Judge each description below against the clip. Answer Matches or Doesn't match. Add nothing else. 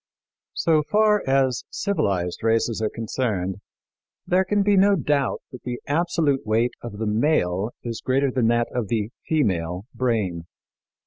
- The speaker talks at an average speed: Matches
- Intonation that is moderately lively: Doesn't match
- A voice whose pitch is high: Doesn't match